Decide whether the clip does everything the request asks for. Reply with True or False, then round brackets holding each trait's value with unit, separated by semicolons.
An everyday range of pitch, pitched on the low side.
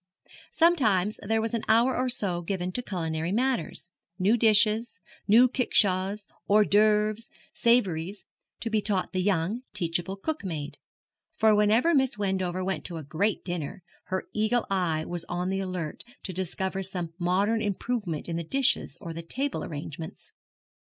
False (4.0 semitones; 195 Hz)